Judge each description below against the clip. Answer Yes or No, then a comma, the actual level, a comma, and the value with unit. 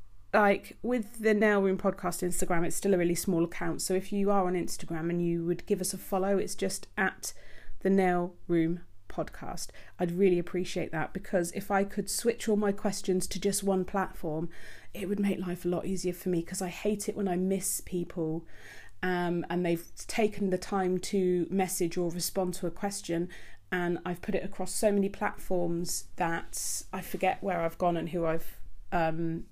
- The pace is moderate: Yes, average, 195 wpm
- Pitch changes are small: Yes, narrow, 2.2 semitones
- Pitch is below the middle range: No, medium, 185 Hz